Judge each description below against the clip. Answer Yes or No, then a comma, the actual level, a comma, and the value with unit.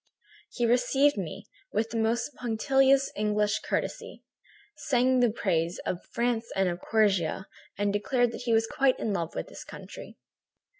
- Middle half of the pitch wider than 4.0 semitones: No, average, 3.3 semitones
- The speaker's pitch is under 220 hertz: No, high, 225 Hz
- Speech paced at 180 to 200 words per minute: No, average, 155 wpm